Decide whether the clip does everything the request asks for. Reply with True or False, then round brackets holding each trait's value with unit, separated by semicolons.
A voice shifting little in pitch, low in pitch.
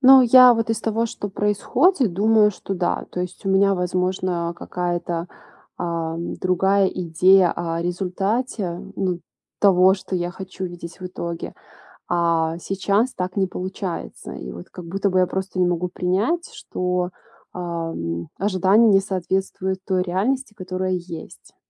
False (2.2 semitones; 185 Hz)